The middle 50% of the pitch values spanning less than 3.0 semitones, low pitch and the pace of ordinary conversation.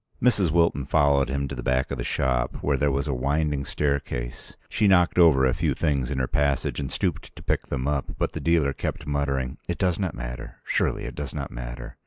No: narrow, 2.4 semitones; very low, 70 Hz; fast, 220 wpm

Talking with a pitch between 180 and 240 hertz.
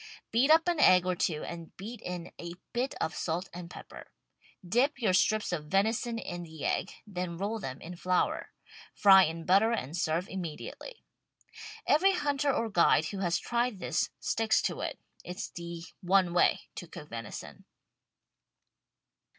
Yes: medium, 185 Hz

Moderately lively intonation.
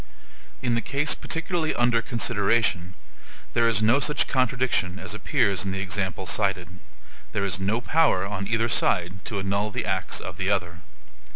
Yes: average, 3.8 semitones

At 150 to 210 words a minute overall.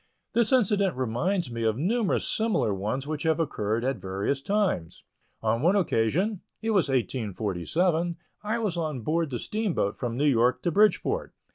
Yes: average, 165 wpm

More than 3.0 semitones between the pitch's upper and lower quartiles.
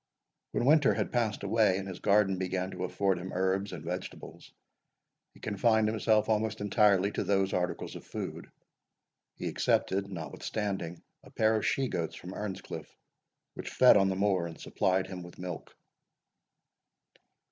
No: narrow, 2.5 semitones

